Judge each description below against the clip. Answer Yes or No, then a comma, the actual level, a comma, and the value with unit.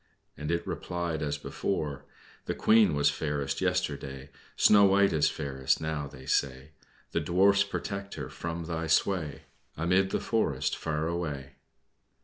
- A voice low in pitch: Yes, very low, 80 Hz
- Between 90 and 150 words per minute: Yes, average, 140 wpm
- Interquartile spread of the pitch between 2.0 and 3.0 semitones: No, average, 3.9 semitones